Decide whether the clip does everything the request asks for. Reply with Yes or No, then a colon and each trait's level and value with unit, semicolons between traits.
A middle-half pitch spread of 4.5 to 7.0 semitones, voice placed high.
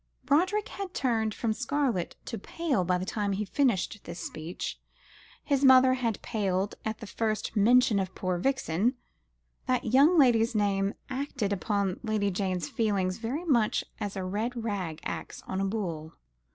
Yes: average, 4.9 semitones; high, 215 Hz